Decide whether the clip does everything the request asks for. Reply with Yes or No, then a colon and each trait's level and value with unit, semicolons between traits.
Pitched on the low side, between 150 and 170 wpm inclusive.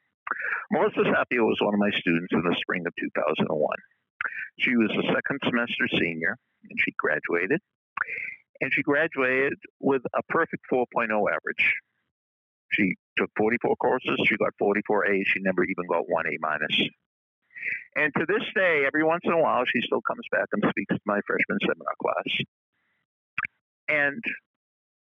Yes: low, 105 Hz; average, 160 wpm